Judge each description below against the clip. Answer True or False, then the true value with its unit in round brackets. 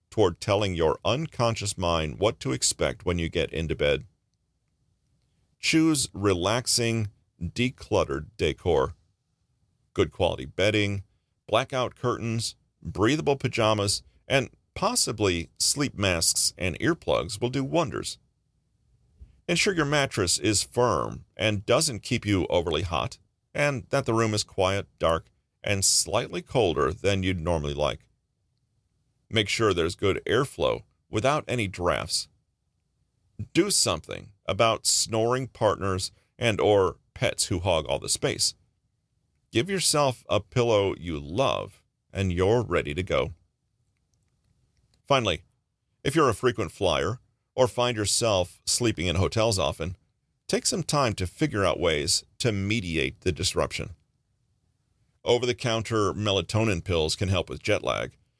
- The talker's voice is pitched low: True (110 Hz)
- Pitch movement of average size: True (4.6 semitones)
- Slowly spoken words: True (125 wpm)